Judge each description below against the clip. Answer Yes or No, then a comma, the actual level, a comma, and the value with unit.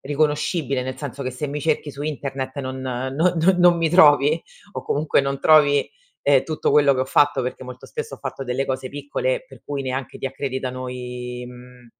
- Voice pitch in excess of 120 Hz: Yes, medium, 140 Hz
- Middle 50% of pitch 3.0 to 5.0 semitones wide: No, narrow, 2.5 semitones